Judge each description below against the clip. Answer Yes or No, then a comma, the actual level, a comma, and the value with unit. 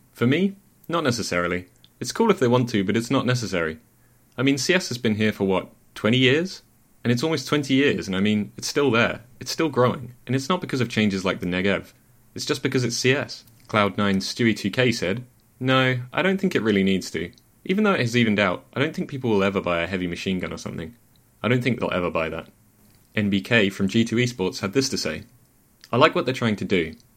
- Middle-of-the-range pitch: No, low, 120 Hz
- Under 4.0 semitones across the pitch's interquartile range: No, average, 4.3 semitones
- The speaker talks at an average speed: No, fast, 230 wpm